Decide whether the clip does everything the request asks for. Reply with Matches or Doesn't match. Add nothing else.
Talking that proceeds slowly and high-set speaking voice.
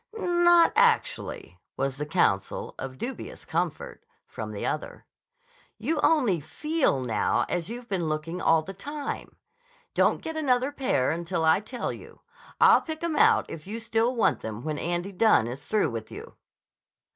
Doesn't match